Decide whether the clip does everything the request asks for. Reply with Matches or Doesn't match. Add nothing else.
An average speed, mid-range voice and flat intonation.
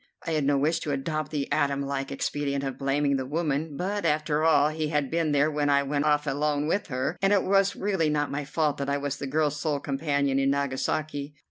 Doesn't match